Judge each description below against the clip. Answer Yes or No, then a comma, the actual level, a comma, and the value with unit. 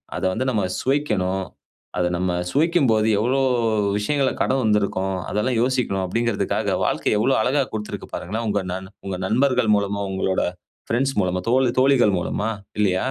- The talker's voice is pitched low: Yes, low, 110 Hz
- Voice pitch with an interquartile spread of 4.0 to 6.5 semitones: Yes, average, 5.1 semitones